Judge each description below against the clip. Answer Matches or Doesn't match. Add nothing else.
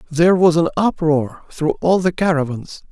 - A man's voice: Matches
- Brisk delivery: Doesn't match